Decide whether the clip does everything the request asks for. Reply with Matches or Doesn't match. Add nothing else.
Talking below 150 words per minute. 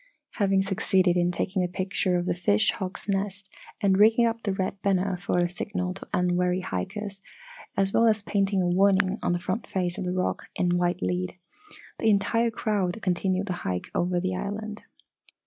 Doesn't match